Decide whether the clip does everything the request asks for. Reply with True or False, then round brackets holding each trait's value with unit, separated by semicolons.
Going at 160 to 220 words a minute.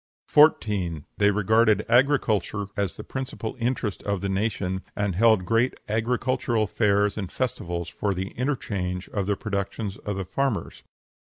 False (140 wpm)